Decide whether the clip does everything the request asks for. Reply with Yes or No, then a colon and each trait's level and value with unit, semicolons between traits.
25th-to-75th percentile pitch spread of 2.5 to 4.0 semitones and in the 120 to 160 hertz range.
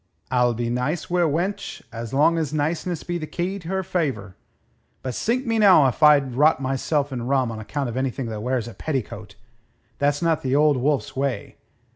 No: average, 4.7 semitones; medium, 140 Hz